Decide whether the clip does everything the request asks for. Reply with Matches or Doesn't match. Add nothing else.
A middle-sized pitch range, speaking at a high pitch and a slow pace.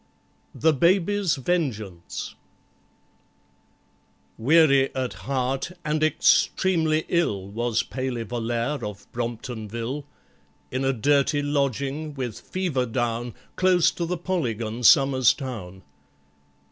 Doesn't match